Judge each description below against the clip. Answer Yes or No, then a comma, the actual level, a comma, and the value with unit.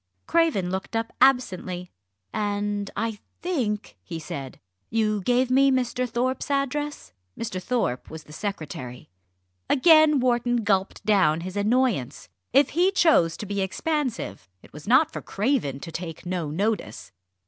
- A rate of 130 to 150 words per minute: Yes, average, 140 wpm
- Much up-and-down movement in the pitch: Yes, wide, 6.3 semitones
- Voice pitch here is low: No, high, 210 Hz